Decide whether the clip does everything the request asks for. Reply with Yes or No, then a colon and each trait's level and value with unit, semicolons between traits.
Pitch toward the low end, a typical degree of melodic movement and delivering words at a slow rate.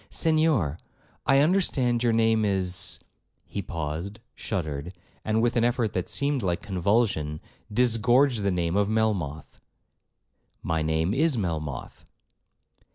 No: low, 105 Hz; wide, 6.1 semitones; slow, 120 wpm